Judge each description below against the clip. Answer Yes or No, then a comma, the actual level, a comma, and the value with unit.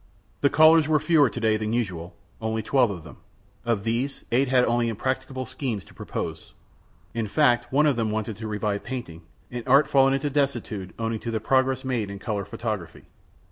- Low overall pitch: Yes, low, 120 Hz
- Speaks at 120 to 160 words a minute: No, average, 190 wpm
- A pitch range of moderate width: Yes, average, 3.8 semitones